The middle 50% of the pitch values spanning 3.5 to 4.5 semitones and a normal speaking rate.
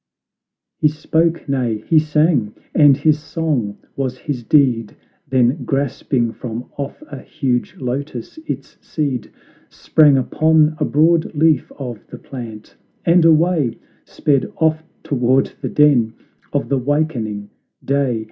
No: average, 4.0 semitones; slow, 130 wpm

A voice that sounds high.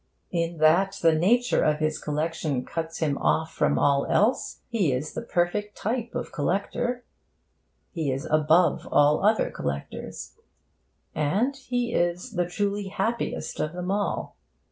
No: medium, 175 Hz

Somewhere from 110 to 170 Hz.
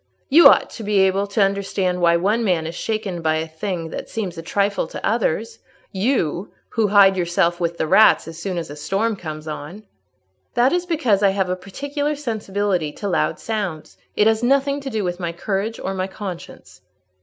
No: high, 195 Hz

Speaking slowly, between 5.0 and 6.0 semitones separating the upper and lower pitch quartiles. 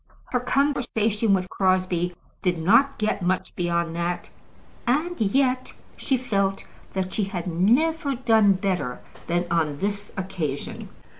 Yes: slow, 130 wpm; wide, 5.6 semitones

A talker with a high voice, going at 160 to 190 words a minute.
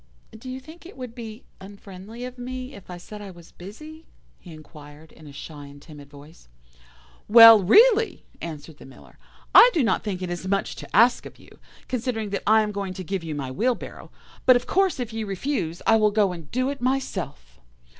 No: high, 205 Hz; fast, 205 wpm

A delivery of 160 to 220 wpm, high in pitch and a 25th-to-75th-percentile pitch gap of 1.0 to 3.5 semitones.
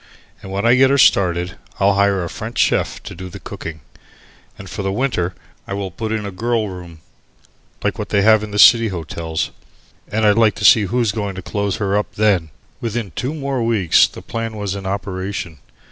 No: fast, 205 wpm; low, 100 Hz; average, 3.1 semitones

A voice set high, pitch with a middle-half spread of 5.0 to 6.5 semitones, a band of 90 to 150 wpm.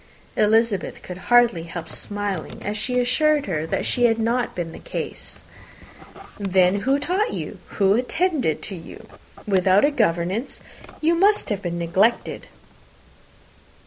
Yes: high, 210 Hz; wide, 5.4 semitones; slow, 135 wpm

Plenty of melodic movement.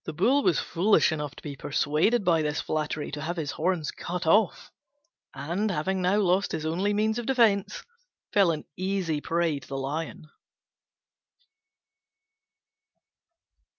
No: average, 4.6 semitones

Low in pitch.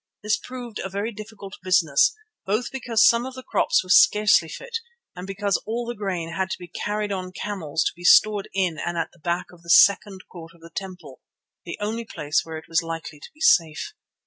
No: high, 190 Hz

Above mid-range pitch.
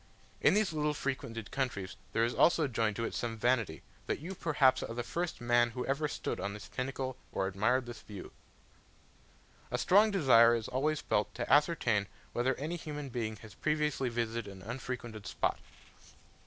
No: low, 125 Hz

